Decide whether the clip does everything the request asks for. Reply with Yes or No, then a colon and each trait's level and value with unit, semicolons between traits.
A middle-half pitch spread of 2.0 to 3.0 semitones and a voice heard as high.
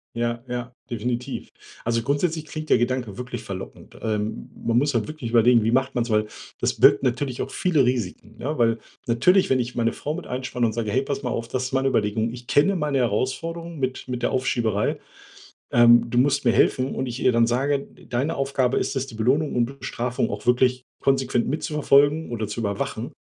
No: average, 2.7 semitones; low, 125 Hz